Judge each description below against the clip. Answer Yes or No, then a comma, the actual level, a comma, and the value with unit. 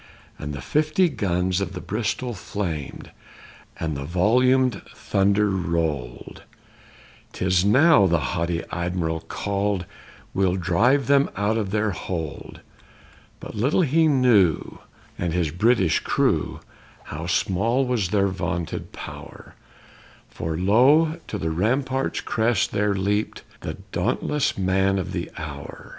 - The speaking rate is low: Yes, slow, 125 wpm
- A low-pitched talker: Yes, low, 100 Hz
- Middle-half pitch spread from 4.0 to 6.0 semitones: Yes, wide, 5.4 semitones